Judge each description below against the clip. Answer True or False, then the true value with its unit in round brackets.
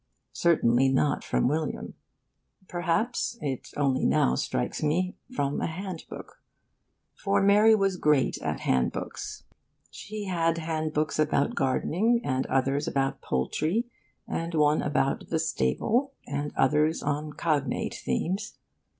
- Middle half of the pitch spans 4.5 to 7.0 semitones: True (4.9 semitones)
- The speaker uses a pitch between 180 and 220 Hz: False (155 Hz)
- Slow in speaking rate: True (120 wpm)